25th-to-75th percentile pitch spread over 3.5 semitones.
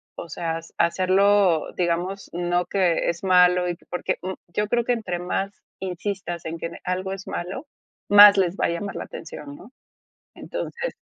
No: narrow, 2.5 semitones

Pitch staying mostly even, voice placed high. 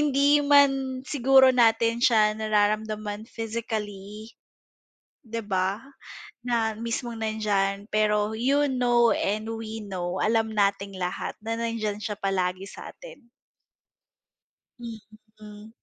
Yes: narrow, 2.2 semitones; high, 220 Hz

